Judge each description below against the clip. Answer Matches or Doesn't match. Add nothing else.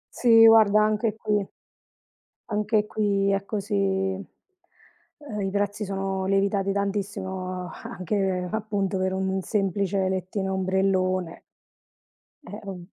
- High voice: Matches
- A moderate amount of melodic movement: Doesn't match